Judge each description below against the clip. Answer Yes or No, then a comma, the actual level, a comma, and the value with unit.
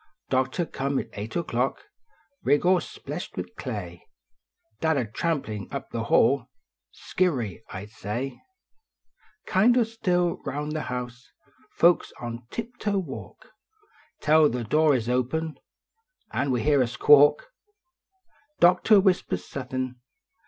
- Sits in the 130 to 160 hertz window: Yes, medium, 140 Hz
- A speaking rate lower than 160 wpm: Yes, slow, 135 wpm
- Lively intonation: Yes, wide, 5.9 semitones